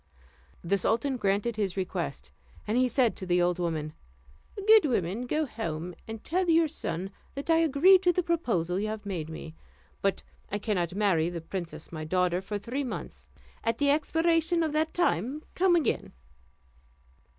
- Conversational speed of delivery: Yes, average, 170 wpm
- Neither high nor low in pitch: No, high, 215 Hz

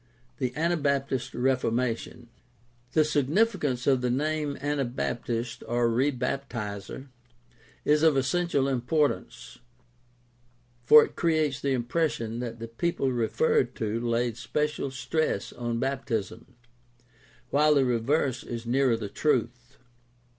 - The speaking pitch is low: Yes, low, 130 Hz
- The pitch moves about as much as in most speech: Yes, average, 3.7 semitones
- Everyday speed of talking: No, slow, 110 wpm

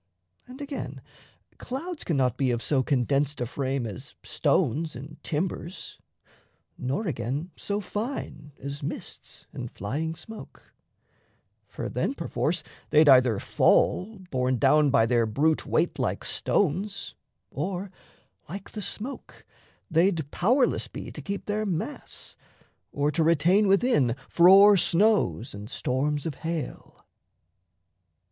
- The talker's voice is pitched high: No, medium, 155 Hz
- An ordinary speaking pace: No, slow, 125 wpm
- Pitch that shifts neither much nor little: No, wide, 6.6 semitones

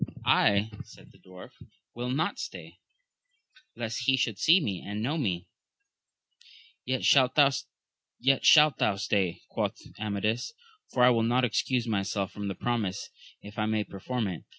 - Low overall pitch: Yes, low, 110 Hz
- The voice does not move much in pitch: No, average, 4.2 semitones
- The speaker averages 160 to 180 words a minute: No, average, 140 wpm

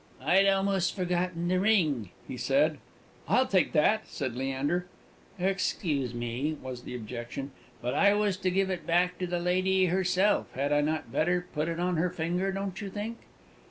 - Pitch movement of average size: Yes, average, 4.5 semitones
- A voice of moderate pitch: Yes, medium, 180 Hz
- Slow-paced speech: No, average, 175 wpm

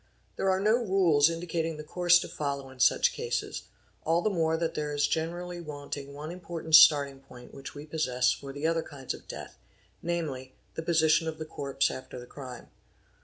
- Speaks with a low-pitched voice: No, medium, 155 Hz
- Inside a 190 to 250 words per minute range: Yes, average, 195 wpm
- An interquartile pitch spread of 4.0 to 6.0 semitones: No, average, 3.2 semitones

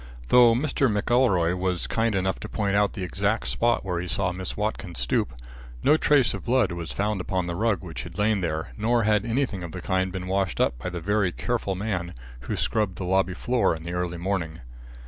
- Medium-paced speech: No, fast, 215 wpm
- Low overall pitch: Yes, very low, 95 Hz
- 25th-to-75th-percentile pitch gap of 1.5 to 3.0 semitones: No, average, 3.7 semitones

